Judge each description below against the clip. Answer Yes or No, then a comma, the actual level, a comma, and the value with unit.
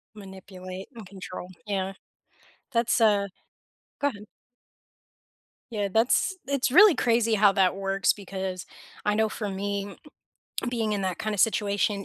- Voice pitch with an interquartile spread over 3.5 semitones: No, narrow, 2.5 semitones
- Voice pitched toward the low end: No, high, 205 Hz